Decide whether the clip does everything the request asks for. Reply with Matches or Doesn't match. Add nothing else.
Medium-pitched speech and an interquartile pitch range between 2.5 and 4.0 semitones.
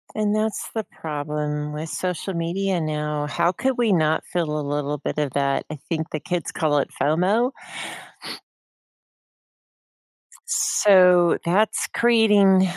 Doesn't match